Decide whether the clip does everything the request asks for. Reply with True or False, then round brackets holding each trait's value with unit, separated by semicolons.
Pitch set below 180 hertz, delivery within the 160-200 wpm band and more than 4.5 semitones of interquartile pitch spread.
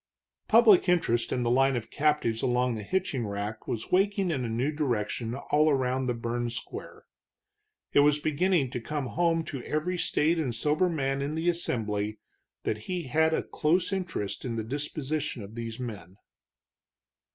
True (135 Hz; 175 wpm; 5.4 semitones)